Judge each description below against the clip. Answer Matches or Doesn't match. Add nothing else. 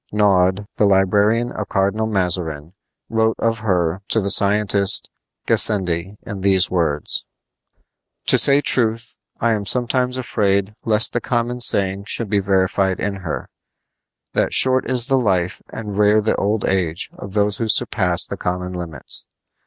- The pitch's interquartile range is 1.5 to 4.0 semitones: Matches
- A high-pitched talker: Doesn't match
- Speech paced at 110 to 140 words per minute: Doesn't match